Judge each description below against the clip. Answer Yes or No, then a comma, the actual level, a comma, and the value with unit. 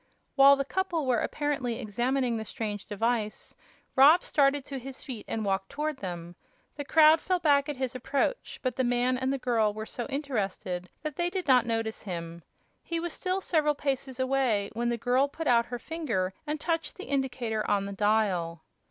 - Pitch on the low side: No, very high, 255 Hz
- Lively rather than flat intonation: No, average, 4.8 semitones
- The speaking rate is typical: Yes, average, 190 wpm